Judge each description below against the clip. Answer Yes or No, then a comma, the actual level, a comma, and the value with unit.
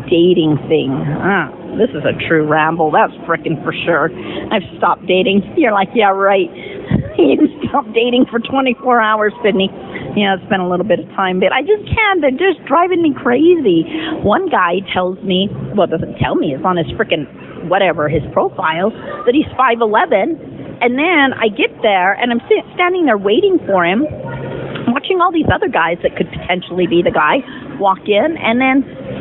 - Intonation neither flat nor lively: No, wide, 8.2 semitones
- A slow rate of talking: No, average, 185 wpm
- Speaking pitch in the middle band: No, high, 225 Hz